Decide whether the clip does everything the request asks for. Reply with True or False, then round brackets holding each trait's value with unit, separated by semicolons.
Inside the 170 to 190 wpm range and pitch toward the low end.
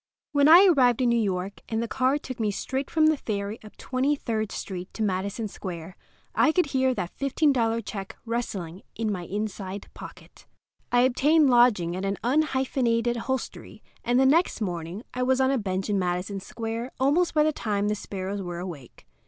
False (185 wpm; 230 Hz)